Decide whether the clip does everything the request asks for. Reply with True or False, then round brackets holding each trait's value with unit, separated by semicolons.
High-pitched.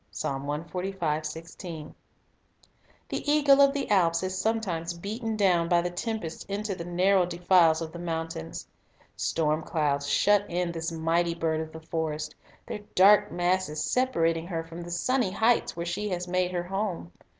False (175 Hz)